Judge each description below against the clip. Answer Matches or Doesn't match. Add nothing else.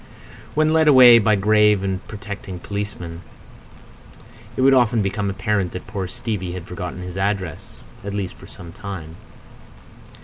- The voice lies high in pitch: Doesn't match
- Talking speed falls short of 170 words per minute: Matches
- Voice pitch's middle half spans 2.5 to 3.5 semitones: Matches